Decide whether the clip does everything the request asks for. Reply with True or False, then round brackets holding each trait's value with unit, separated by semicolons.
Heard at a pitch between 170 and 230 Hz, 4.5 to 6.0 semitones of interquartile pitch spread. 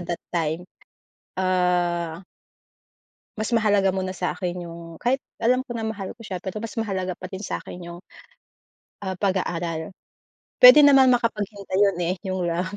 False (190 Hz; 3.6 semitones)